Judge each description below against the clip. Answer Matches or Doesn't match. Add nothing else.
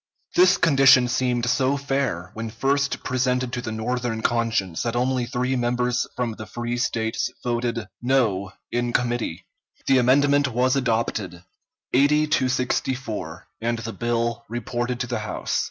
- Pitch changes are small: Matches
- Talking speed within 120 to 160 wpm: Matches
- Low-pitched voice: Matches